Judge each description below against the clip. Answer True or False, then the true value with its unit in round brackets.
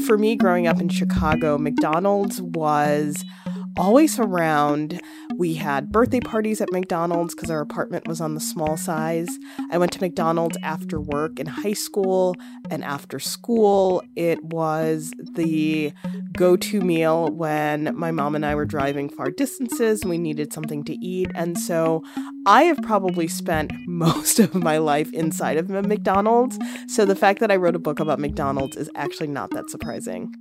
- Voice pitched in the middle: True (180 Hz)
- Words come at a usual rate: True (170 wpm)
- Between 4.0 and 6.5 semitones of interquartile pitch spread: True (5.2 semitones)